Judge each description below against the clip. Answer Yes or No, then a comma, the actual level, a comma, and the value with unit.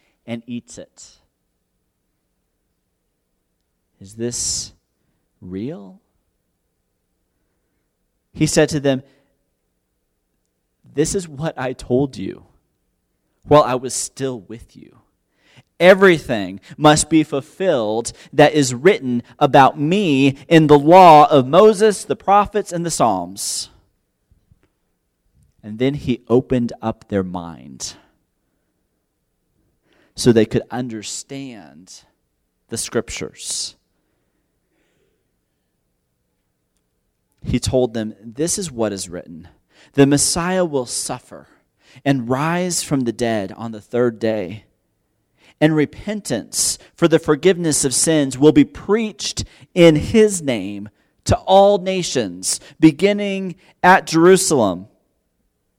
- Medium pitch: No, low, 125 Hz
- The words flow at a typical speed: No, slow, 100 wpm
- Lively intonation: Yes, wide, 8.5 semitones